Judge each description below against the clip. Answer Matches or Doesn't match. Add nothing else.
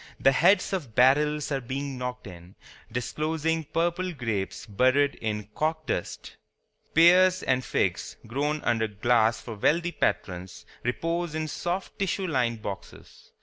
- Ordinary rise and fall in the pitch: Doesn't match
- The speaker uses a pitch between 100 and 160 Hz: Matches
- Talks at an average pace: Doesn't match